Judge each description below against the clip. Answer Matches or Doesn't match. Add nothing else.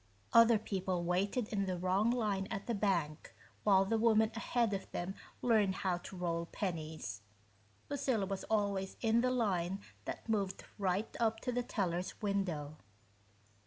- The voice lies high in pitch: Matches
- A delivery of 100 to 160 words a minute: Matches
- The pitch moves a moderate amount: Matches